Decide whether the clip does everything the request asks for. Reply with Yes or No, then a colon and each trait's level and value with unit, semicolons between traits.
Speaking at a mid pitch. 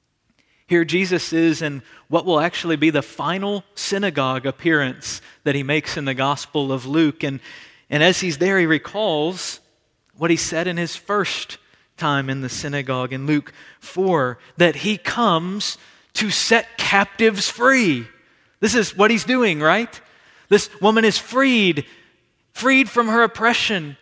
Yes: medium, 170 Hz